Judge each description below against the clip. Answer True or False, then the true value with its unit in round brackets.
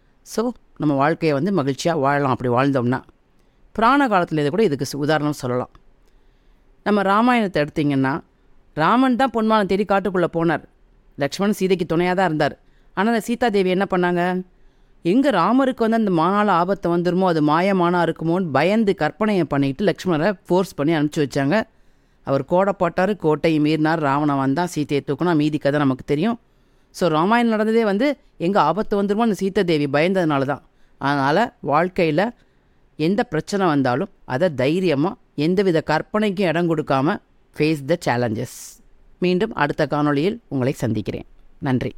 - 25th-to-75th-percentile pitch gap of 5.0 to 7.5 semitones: True (5.4 semitones)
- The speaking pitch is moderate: True (170 Hz)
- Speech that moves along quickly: True (135 wpm)